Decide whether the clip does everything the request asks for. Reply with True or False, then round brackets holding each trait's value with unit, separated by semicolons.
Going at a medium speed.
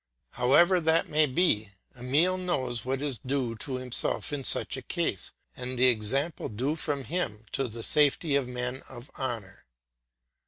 True (160 wpm)